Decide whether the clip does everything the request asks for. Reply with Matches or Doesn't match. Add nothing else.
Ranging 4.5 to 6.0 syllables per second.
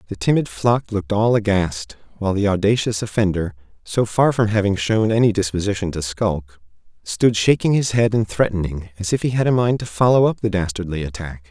Matches